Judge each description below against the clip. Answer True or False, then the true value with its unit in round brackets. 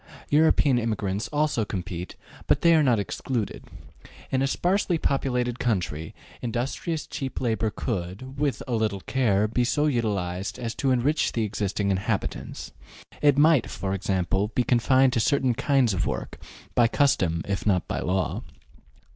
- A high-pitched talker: False (120 Hz)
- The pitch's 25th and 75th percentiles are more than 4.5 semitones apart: True (5.4 semitones)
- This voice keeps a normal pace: True (150 wpm)